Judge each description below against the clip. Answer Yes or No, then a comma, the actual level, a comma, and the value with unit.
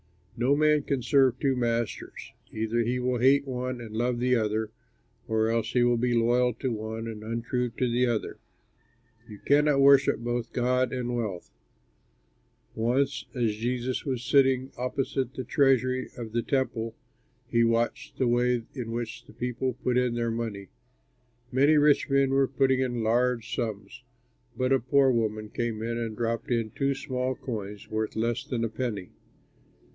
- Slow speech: No, average, 165 wpm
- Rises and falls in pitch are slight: Yes, narrow, 2.1 semitones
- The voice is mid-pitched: No, low, 120 Hz